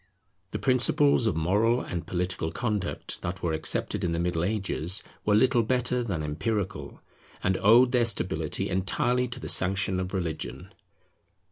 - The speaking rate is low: No, average, 150 wpm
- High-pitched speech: No, low, 100 Hz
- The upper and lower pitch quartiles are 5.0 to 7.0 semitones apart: Yes, wide, 5.4 semitones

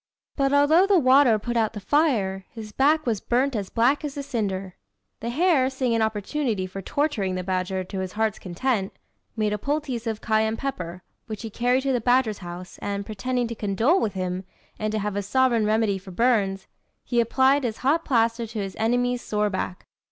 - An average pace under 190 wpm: No, average, 200 wpm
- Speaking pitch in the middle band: No, high, 225 Hz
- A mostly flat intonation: No, average, 4.6 semitones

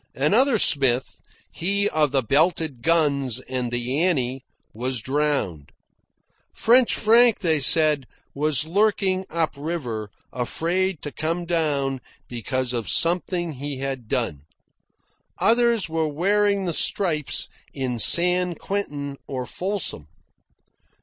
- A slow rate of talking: Yes, slow, 115 wpm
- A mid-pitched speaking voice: Yes, medium, 155 Hz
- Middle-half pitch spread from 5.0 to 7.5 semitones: Yes, wide, 5.5 semitones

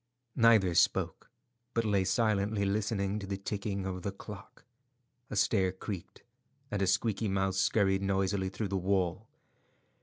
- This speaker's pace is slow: No, average, 145 wpm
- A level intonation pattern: Yes, narrow, 1.7 semitones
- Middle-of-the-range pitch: No, low, 100 Hz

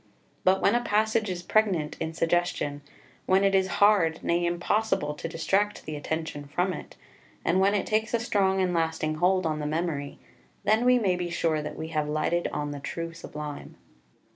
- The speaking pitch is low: No, medium, 175 Hz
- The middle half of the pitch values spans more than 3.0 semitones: Yes, average, 4.1 semitones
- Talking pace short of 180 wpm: No, average, 190 wpm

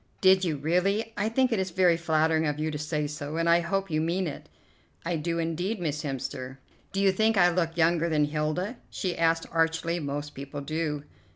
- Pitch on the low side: No, medium, 165 Hz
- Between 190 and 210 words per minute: Yes, fast, 205 wpm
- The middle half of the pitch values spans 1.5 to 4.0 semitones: Yes, average, 3.1 semitones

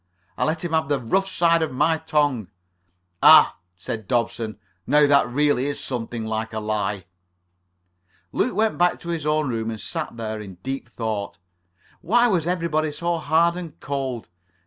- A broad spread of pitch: Yes, wide, 6.5 semitones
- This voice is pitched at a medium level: Yes, medium, 145 Hz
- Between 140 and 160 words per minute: No, average, 170 wpm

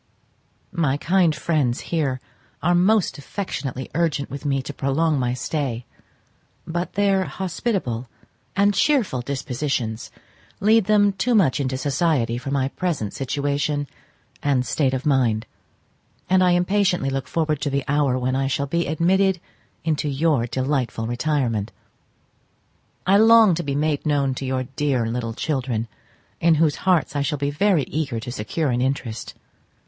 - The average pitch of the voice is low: No, medium, 145 Hz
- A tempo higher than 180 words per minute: No, average, 150 wpm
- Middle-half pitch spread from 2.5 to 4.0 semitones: No, average, 4.7 semitones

